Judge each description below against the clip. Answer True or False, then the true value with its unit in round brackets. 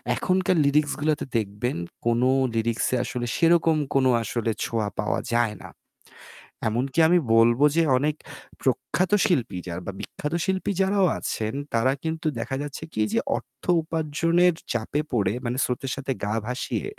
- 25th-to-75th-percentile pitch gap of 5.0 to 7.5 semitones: True (5.6 semitones)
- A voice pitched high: False (130 Hz)